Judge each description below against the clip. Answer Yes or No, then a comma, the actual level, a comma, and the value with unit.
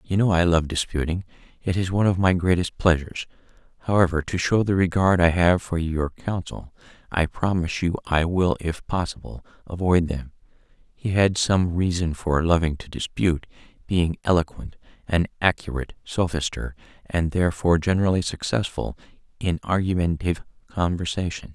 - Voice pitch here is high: No, very low, 90 Hz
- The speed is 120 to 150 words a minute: Yes, average, 140 wpm